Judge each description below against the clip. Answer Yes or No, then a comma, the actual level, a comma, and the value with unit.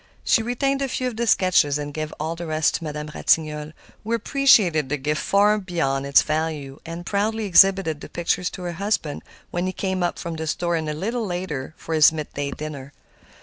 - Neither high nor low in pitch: Yes, medium, 165 Hz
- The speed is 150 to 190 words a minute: No, average, 200 wpm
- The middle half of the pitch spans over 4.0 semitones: Yes, average, 4.6 semitones